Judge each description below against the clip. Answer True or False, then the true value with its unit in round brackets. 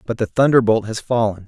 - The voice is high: False (115 Hz)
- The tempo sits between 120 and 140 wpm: False (205 wpm)